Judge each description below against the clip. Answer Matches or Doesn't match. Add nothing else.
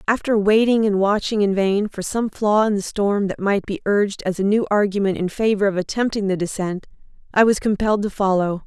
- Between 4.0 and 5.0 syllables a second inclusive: Doesn't match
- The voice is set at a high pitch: Matches